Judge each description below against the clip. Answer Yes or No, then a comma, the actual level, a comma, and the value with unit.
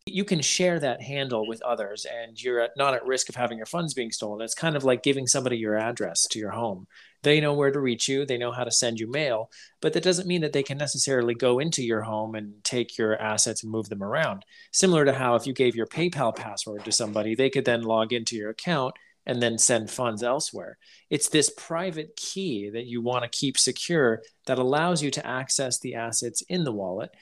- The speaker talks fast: Yes, fast, 230 wpm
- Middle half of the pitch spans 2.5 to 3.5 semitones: No, average, 4.2 semitones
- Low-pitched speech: Yes, low, 125 Hz